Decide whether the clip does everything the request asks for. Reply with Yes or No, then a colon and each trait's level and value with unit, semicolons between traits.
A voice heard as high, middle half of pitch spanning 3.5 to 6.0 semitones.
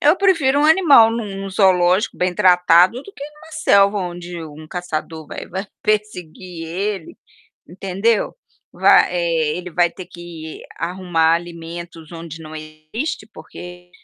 No: medium, 180 Hz; average, 3.9 semitones